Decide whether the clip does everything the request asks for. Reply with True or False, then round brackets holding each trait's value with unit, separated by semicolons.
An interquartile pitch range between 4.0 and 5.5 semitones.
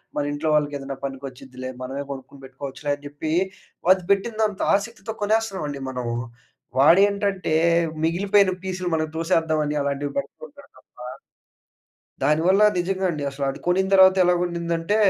True (5.2 semitones)